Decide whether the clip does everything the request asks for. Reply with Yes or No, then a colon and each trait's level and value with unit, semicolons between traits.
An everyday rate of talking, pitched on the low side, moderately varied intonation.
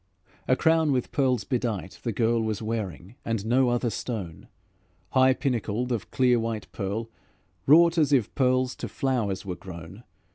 Yes: average, 155 wpm; low, 120 Hz; average, 3.9 semitones